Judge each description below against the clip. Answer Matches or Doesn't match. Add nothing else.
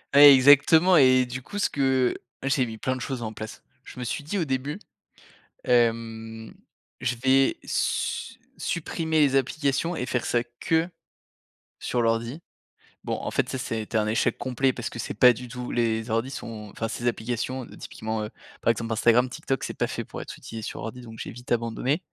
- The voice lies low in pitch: Matches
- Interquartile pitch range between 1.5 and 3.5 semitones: Matches